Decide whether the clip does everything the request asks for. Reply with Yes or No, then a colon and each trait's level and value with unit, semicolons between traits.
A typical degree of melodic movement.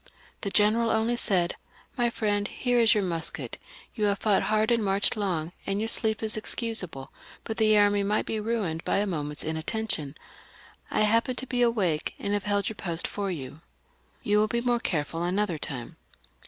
Yes: average, 4.3 semitones